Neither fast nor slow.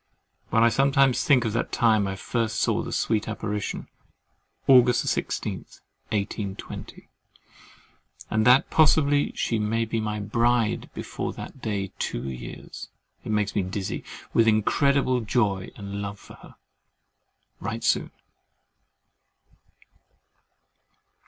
No: slow, 120 wpm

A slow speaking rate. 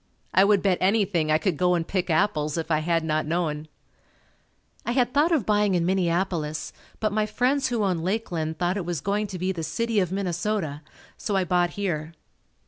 No: average, 200 wpm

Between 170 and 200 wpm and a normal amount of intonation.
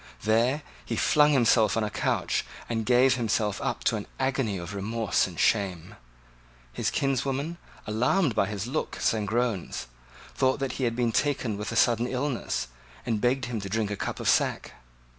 Yes: average, 175 wpm; average, 3.7 semitones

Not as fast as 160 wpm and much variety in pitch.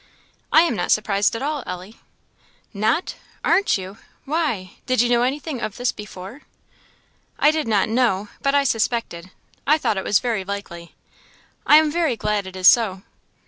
No: average, 170 wpm; wide, 5.9 semitones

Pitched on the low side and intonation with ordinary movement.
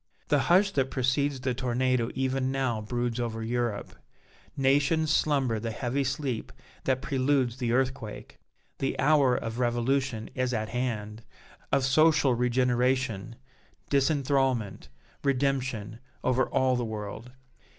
No: low, 130 Hz; narrow, 2.3 semitones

